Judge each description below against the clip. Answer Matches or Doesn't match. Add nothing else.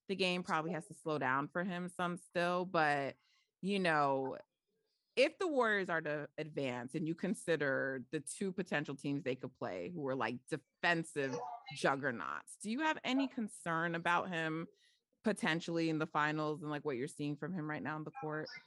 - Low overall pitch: Doesn't match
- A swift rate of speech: Doesn't match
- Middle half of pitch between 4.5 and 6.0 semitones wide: Doesn't match